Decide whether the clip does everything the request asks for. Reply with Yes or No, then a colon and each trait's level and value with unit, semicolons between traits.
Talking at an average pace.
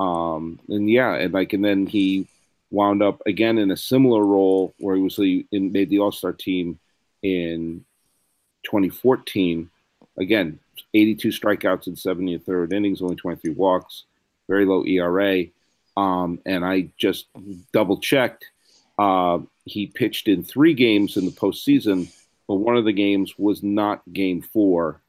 Yes: average, 160 wpm